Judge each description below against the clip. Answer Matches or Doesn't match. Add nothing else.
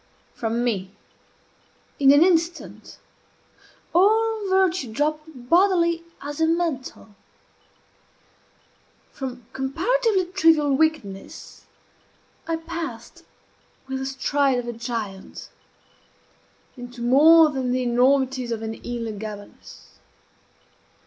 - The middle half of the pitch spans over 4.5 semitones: Matches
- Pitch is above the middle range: Matches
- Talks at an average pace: Doesn't match